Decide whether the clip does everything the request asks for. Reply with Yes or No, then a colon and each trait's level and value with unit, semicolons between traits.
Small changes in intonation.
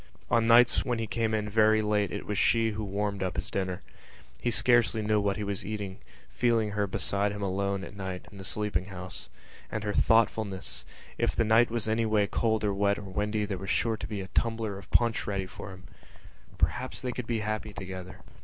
Yes: narrow, 2.2 semitones